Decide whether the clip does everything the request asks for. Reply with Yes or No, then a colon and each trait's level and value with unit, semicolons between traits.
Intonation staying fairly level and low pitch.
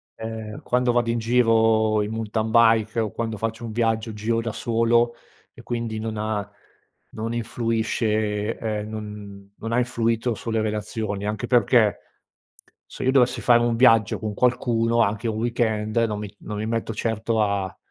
Yes: narrow, 1.5 semitones; low, 110 Hz